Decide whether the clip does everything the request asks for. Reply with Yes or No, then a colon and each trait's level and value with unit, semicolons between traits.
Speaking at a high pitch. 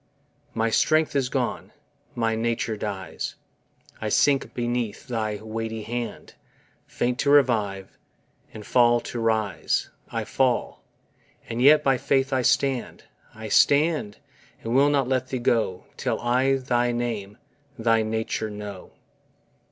No: low, 120 Hz